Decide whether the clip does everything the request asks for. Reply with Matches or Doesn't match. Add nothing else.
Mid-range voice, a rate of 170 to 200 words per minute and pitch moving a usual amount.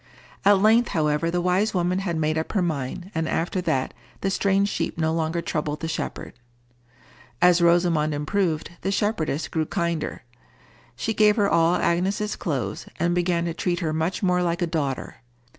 Matches